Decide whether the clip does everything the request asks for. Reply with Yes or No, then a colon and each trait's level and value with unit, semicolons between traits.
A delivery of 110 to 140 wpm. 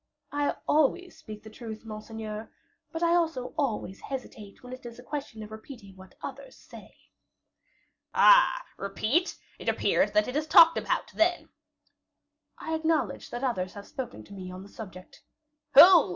No: average, 160 wpm